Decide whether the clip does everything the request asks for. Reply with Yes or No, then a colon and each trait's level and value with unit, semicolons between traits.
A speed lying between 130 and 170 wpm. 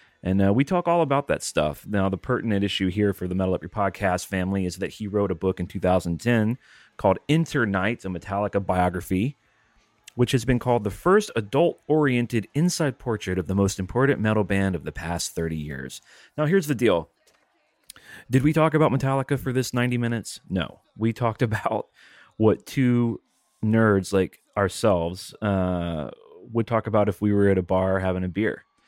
No: average, 185 wpm